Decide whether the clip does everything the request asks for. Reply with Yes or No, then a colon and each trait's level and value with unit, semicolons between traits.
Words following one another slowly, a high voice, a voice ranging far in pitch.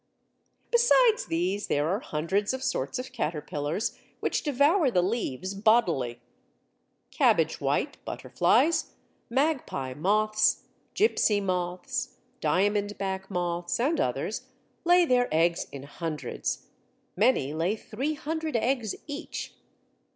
Yes: slow, 105 wpm; high, 205 Hz; wide, 7.3 semitones